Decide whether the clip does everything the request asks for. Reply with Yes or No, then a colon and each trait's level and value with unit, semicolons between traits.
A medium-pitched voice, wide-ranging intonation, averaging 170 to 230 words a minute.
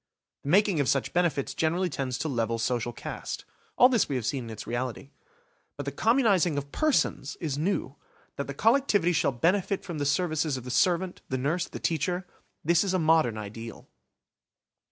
Yes: medium, 155 Hz; wide, 5.8 semitones; average, 180 wpm